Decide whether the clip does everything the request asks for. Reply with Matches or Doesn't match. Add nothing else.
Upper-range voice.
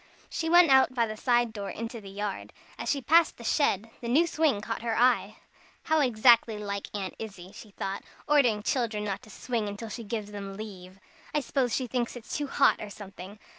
Matches